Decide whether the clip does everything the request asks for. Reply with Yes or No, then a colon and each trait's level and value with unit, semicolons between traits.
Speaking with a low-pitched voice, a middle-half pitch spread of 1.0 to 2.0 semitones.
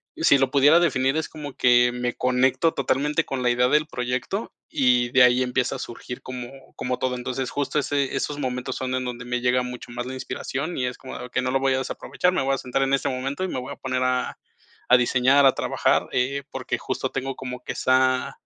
Yes: low, 130 Hz; narrow, 1.5 semitones